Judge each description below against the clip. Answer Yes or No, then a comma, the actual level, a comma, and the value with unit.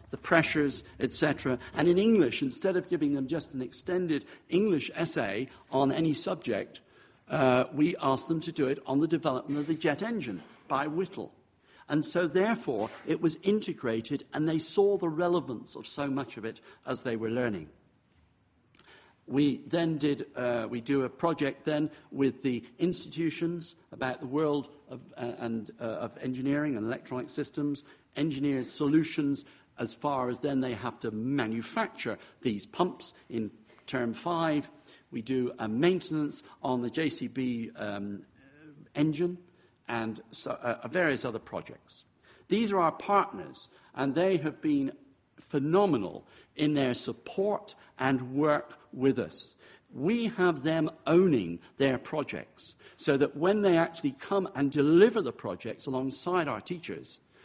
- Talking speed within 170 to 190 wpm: No, average, 150 wpm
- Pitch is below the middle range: No, medium, 145 Hz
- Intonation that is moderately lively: Yes, average, 4.5 semitones